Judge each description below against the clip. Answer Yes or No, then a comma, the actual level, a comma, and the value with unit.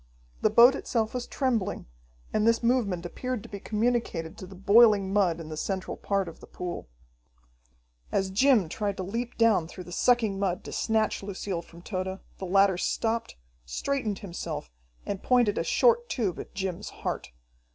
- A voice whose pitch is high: Yes, high, 200 Hz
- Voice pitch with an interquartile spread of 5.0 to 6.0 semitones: No, average, 3.9 semitones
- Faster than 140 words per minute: Yes, average, 170 wpm